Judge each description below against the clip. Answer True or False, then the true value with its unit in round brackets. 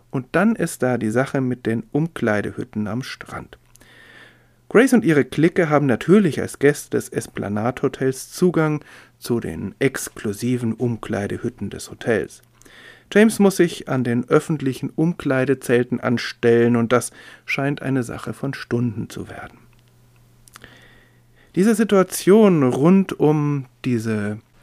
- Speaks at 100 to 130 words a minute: True (125 wpm)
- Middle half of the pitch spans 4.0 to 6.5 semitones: True (4.3 semitones)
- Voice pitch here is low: True (130 Hz)